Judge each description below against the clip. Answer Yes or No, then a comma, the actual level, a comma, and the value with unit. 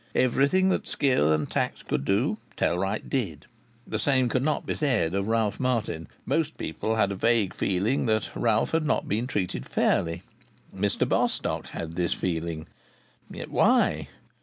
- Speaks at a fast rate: No, average, 160 wpm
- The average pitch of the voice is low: Yes, low, 105 Hz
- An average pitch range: No, wide, 6.5 semitones